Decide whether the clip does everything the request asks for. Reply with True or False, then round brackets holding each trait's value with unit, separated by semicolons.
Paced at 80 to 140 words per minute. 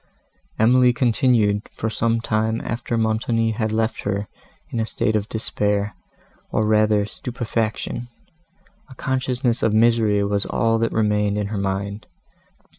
True (135 wpm)